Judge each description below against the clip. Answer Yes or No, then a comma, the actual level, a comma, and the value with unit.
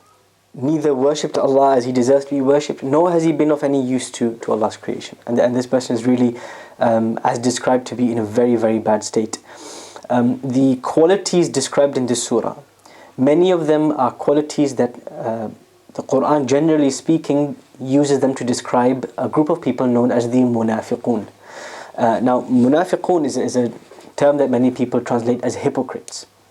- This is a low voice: Yes, low, 130 Hz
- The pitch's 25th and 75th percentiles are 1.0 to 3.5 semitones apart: Yes, average, 2.9 semitones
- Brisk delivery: No, average, 180 wpm